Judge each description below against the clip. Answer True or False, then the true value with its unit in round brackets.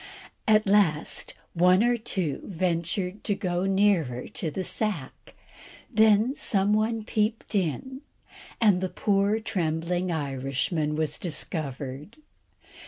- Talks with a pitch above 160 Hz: True (185 Hz)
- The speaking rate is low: True (110 wpm)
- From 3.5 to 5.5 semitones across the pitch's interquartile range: True (4.9 semitones)